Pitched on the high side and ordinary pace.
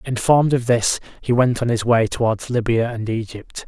No: low, 120 Hz; average, 195 wpm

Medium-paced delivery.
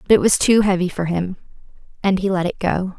No: fast, 240 wpm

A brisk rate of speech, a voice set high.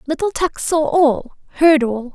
No: average, 170 wpm; very high, 290 Hz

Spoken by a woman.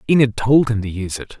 No: male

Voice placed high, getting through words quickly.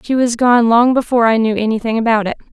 Yes: high, 230 Hz; fast, 255 wpm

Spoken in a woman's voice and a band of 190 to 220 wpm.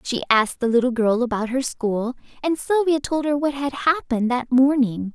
Yes: female; average, 200 wpm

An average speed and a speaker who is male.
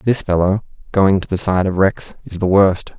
Yes: average, 180 wpm; male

